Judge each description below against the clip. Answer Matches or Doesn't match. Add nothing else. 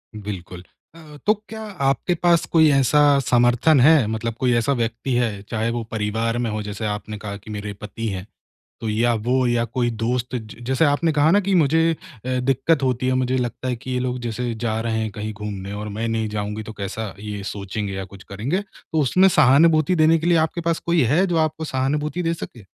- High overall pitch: Doesn't match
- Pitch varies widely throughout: Matches